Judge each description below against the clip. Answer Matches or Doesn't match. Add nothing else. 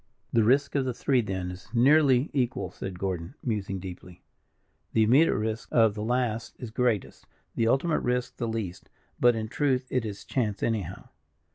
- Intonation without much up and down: Doesn't match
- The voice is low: Matches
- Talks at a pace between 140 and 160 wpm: Doesn't match